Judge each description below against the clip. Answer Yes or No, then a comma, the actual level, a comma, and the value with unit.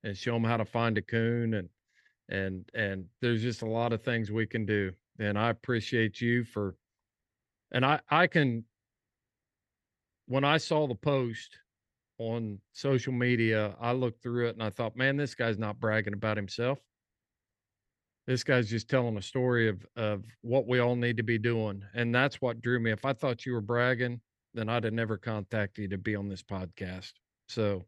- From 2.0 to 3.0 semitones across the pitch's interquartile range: Yes, narrow, 2.6 semitones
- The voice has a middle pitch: No, low, 115 Hz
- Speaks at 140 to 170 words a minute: No, average, 190 wpm